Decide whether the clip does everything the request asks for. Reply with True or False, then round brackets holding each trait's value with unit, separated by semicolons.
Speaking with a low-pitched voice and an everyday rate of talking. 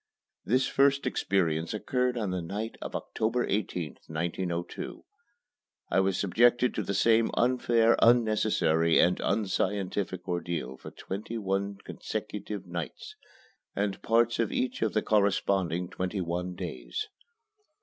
False (100 Hz; 125 wpm)